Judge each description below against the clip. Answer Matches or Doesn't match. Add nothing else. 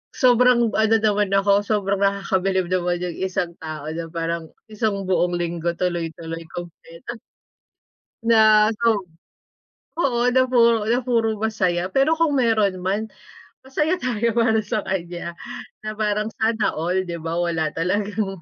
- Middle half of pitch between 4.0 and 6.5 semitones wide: Matches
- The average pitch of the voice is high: Matches